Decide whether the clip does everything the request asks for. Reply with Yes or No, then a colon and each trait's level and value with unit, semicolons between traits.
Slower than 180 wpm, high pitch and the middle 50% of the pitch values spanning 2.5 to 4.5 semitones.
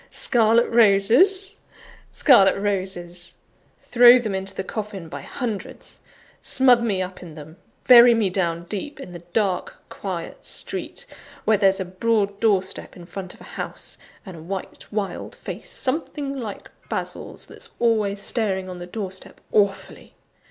Yes: average, 150 wpm; high, 200 Hz; average, 3.9 semitones